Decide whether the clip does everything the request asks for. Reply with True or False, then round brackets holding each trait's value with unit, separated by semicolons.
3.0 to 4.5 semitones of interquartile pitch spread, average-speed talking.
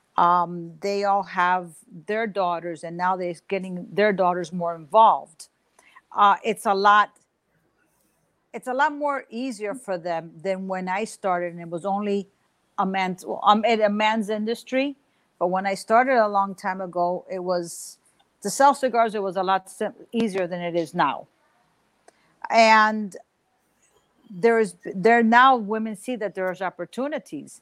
True (3.7 semitones; 160 wpm)